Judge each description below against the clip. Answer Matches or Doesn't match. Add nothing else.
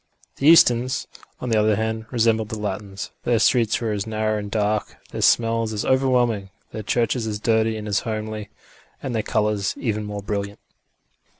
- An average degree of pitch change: Doesn't match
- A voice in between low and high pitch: Doesn't match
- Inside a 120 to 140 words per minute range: Doesn't match